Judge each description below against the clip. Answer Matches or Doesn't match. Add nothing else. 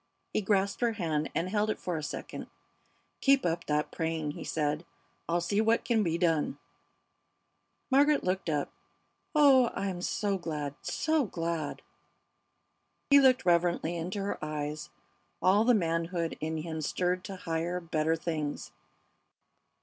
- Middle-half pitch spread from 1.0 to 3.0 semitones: Doesn't match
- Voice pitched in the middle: Matches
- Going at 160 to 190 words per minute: Doesn't match